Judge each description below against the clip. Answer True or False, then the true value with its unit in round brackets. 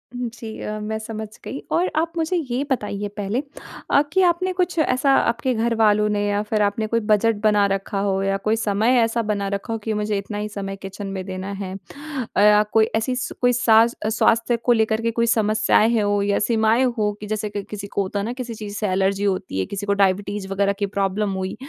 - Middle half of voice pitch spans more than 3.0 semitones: False (2.4 semitones)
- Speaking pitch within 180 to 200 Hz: False (215 Hz)